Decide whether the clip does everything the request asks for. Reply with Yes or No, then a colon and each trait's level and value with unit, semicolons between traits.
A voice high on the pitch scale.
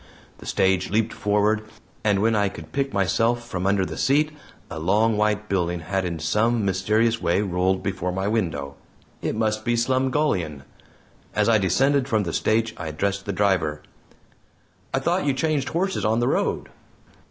No: low, 105 Hz